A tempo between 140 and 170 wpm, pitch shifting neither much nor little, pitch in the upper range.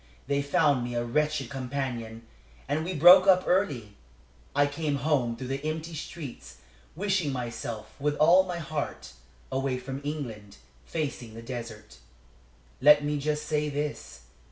No: average, 145 wpm; average, 3.9 semitones; medium, 145 Hz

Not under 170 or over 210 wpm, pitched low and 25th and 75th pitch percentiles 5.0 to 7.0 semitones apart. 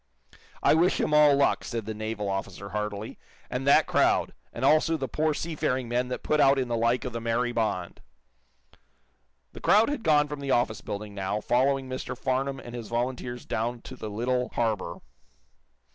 No: average, 185 wpm; low, 125 Hz; average, 3.9 semitones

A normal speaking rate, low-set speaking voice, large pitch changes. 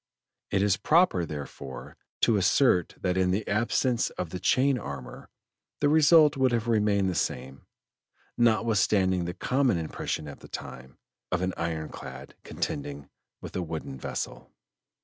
Yes: average, 150 wpm; very low, 95 Hz; wide, 7.0 semitones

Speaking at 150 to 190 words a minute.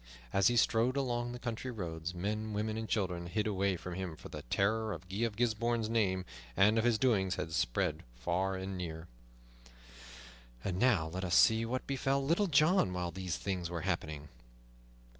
Yes: average, 180 wpm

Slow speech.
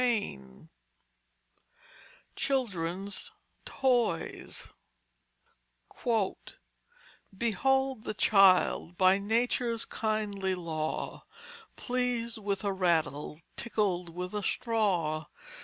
Yes: slow, 75 wpm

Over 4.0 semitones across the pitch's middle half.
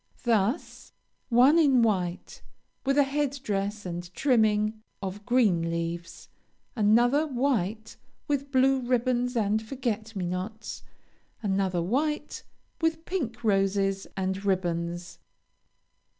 Yes: average, 5.1 semitones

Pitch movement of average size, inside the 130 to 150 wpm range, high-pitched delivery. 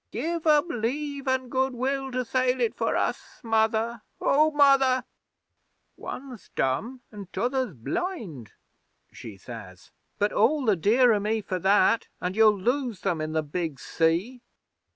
No: wide, 5.9 semitones; average, 145 wpm; high, 230 Hz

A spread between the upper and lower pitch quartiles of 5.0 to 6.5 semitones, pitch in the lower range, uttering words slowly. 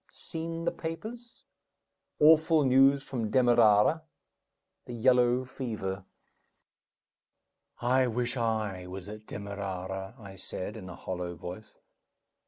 Yes: wide, 5.5 semitones; low, 115 Hz; slow, 110 wpm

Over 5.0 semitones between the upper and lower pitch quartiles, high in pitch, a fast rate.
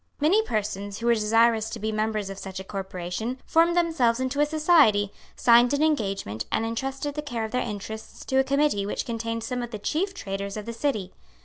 Yes: wide, 5.4 semitones; high, 230 Hz; fast, 210 wpm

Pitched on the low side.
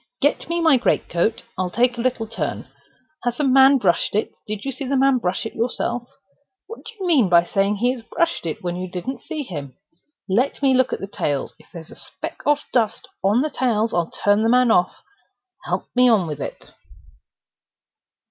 No: high, 235 Hz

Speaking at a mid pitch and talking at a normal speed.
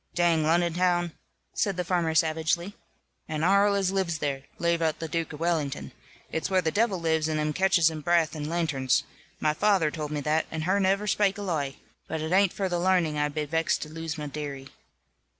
No: medium, 165 Hz; fast, 210 wpm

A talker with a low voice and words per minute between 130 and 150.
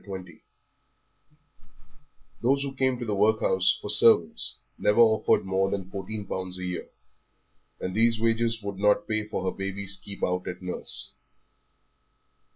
Yes: low, 100 Hz; average, 145 wpm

